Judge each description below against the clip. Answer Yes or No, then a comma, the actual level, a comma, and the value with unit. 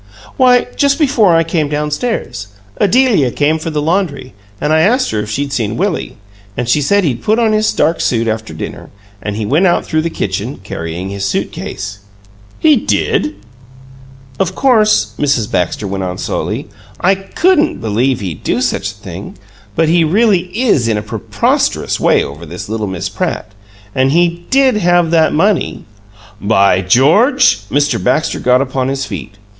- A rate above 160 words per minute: Yes, average, 175 wpm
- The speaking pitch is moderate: Yes, medium, 145 Hz